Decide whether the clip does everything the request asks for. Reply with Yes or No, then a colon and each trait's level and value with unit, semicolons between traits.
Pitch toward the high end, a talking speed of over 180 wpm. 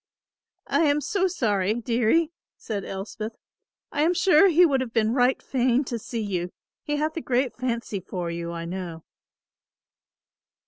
No: high, 240 Hz; average, 155 wpm